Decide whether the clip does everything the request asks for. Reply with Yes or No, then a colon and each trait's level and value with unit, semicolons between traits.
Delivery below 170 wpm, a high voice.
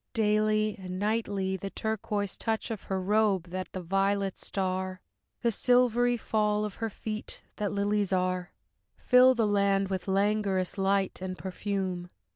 Yes: average, 145 wpm; high, 200 Hz